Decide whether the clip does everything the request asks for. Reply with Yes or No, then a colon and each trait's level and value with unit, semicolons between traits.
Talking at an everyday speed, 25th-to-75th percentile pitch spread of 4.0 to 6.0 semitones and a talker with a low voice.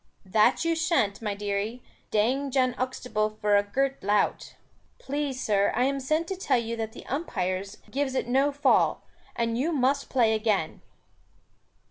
No: average, 160 wpm; average, 4.6 semitones; high, 245 Hz